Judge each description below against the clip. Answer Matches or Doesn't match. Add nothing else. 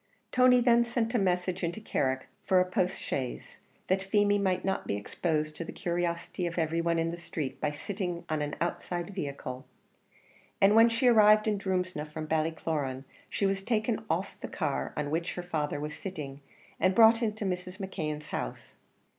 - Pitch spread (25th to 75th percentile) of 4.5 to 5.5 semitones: Matches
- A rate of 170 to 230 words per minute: Matches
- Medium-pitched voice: Matches